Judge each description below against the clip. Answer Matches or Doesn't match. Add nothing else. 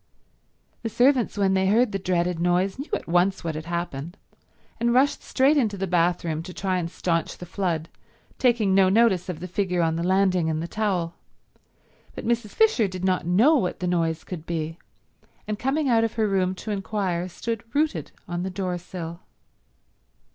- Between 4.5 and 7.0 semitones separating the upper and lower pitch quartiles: Doesn't match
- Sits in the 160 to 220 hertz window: Matches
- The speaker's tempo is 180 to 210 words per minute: Matches